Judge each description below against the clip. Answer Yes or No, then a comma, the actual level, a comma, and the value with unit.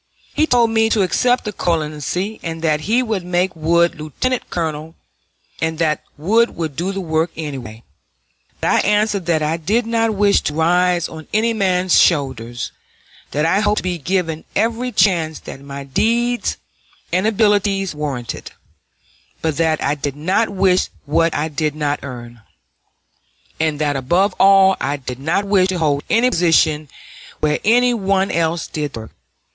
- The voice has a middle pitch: Yes, medium, 170 Hz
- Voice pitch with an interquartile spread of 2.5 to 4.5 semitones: No, average, 4.9 semitones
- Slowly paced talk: No, average, 165 wpm